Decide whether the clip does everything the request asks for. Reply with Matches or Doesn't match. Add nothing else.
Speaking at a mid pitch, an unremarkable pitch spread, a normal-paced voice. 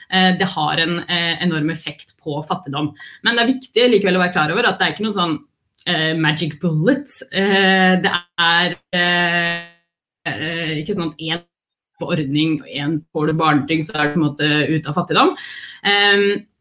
Matches